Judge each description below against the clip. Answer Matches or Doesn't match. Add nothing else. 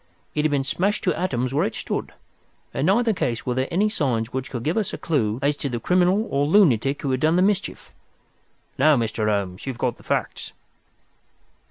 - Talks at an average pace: Doesn't match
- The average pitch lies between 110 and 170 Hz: Matches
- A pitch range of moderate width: Doesn't match